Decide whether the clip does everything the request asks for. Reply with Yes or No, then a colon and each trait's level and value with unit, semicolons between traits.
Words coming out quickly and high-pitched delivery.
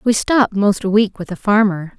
Yes: fast, 240 wpm; high, 205 Hz